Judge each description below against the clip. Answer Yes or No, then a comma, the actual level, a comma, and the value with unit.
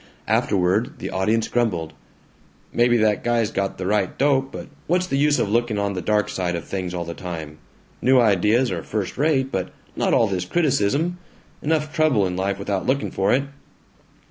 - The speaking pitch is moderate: No, low, 105 Hz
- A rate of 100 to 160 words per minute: No, average, 185 wpm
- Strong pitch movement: Yes, wide, 5.9 semitones